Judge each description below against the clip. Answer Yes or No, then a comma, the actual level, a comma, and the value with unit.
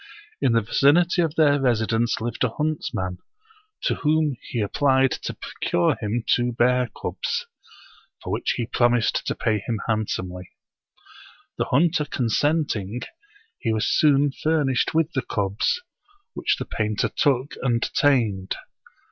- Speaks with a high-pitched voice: No, low, 125 Hz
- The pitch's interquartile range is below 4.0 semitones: No, average, 4.8 semitones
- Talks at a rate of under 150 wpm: Yes, average, 140 wpm